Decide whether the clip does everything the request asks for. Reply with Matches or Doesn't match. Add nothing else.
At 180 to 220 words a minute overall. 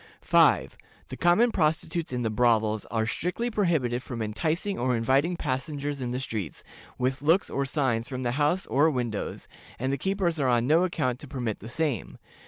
Matches